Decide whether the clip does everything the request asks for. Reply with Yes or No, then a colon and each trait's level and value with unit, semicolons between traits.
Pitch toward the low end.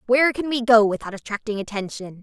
No: high, 225 Hz